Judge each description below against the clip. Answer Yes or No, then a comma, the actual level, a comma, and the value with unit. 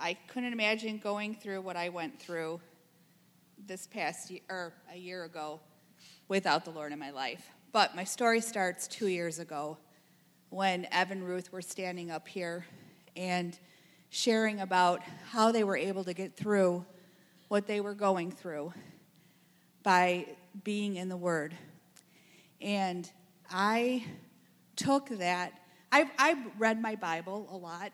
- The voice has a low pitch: No, medium, 180 Hz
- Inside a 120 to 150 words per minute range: Yes, average, 145 wpm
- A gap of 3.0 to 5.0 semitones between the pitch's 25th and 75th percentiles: No, narrow, 2.4 semitones